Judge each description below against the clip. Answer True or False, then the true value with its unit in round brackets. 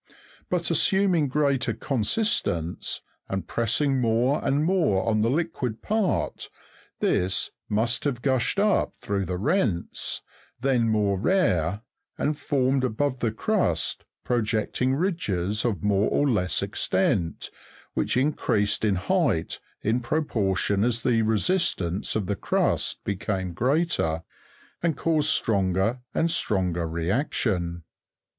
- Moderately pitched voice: False (115 Hz)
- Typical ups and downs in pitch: False (6.8 semitones)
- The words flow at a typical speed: False (120 wpm)